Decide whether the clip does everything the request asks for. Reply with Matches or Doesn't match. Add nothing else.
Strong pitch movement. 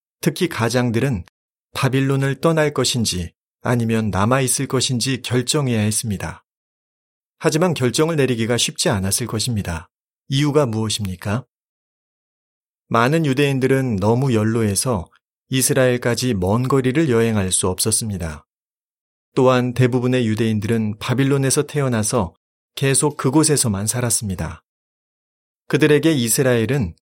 Doesn't match